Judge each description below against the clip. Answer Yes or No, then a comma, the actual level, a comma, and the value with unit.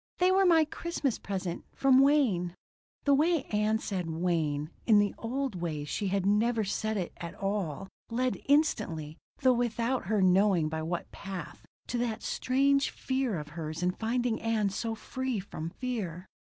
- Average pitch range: No, wide, 6.2 semitones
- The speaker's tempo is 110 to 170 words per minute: Yes, average, 165 wpm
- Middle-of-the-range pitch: No, high, 210 Hz